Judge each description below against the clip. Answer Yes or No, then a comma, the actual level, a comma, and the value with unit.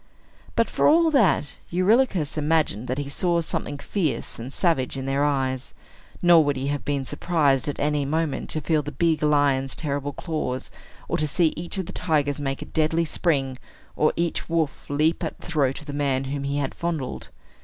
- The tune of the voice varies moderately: Yes, average, 3.1 semitones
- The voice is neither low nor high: Yes, medium, 145 Hz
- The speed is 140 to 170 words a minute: No, average, 195 wpm